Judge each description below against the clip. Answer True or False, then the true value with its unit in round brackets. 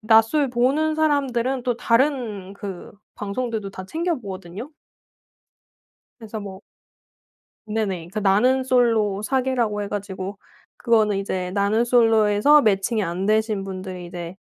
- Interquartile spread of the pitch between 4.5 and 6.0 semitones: False (4.1 semitones)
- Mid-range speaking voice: False (215 Hz)